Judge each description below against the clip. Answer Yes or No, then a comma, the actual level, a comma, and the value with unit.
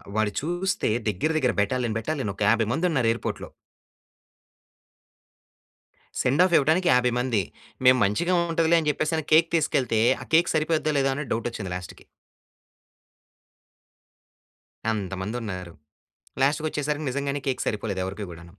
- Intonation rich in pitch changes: Yes, wide, 6.6 semitones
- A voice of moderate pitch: No, low, 130 Hz